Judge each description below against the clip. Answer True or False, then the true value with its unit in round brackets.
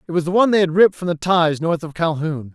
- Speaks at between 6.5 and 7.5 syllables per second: True (6.7 syllables/s)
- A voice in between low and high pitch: True (170 Hz)